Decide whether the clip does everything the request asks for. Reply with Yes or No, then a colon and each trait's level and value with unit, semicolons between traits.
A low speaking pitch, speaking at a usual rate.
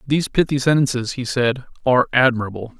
Yes: low, 130 Hz; average, 150 wpm